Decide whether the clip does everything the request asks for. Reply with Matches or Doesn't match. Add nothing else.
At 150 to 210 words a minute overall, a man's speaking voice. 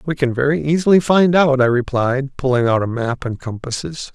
Matches